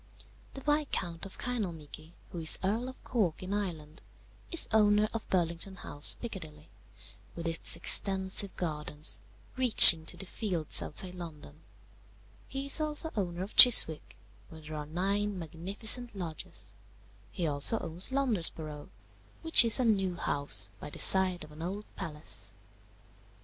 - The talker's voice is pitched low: No, medium, 180 Hz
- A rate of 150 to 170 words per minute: No, average, 140 wpm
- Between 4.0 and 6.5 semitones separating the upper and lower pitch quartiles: Yes, average, 5.1 semitones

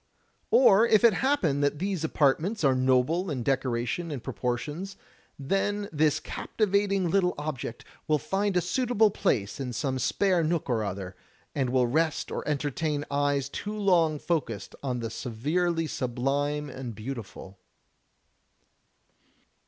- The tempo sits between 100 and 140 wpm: Yes, slow, 135 wpm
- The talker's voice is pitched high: No, medium, 150 Hz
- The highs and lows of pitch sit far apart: Yes, wide, 6.1 semitones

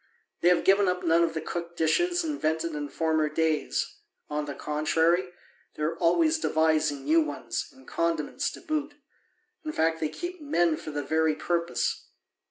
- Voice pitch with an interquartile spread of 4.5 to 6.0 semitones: No, average, 2.8 semitones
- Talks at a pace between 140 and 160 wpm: No, average, 170 wpm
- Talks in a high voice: No, medium, 165 Hz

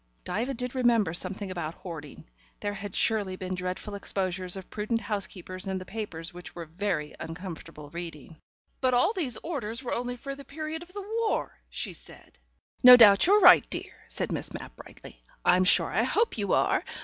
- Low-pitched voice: No, high, 200 Hz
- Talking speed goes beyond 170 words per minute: Yes, average, 185 wpm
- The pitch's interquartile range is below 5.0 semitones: No, wide, 5.5 semitones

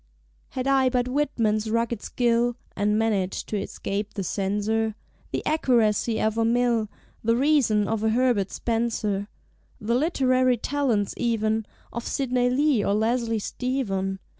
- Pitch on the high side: Yes, high, 230 Hz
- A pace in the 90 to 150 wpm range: Yes, average, 140 wpm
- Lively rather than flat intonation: No, average, 3.0 semitones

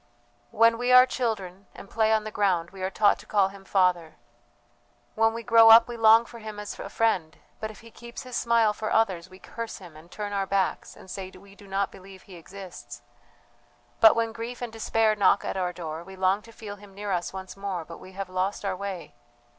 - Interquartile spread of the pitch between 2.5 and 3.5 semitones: Yes, average, 3.2 semitones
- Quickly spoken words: Yes, fast, 225 wpm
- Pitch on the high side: Yes, high, 200 Hz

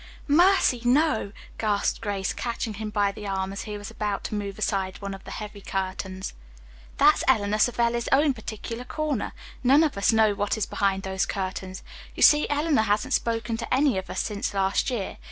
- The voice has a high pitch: Yes, high, 210 Hz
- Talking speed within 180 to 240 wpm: Yes, average, 190 wpm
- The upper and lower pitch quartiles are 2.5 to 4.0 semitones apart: Yes, average, 3.5 semitones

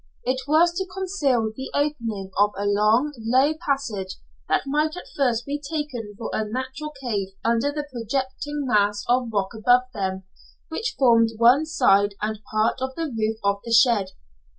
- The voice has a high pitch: Yes, high, 245 Hz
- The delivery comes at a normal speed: Yes, average, 170 wpm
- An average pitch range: Yes, average, 5.0 semitones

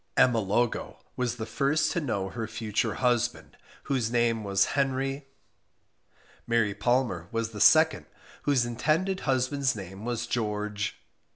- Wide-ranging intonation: No, average, 3.9 semitones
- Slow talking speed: Yes, slow, 130 wpm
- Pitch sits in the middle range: No, low, 120 Hz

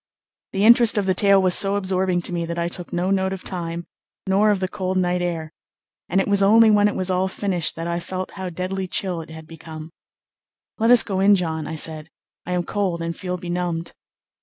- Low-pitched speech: No, medium, 185 Hz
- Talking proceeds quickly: Yes, fast, 225 wpm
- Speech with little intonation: Yes, narrow, 2.3 semitones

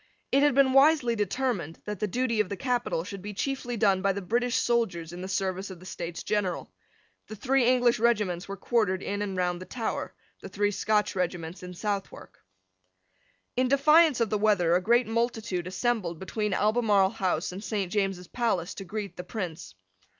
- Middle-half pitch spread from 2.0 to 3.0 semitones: No, average, 4.4 semitones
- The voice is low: No, high, 205 Hz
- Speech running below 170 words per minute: No, average, 185 wpm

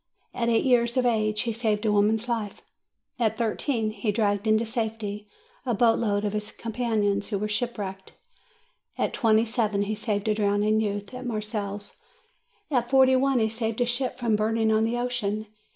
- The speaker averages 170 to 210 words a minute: Yes, average, 180 wpm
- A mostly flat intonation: Yes, narrow, 2.1 semitones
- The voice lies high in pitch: Yes, high, 220 Hz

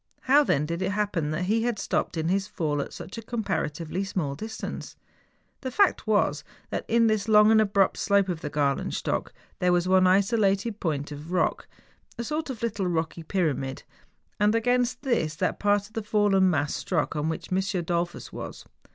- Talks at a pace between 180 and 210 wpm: Yes, average, 185 wpm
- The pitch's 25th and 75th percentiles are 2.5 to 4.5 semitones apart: No, average, 5.0 semitones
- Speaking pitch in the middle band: No, high, 195 Hz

